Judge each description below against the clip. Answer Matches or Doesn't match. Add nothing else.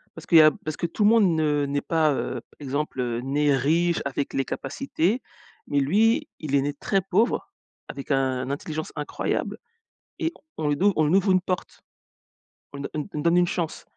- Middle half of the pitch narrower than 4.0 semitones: Doesn't match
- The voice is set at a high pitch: Doesn't match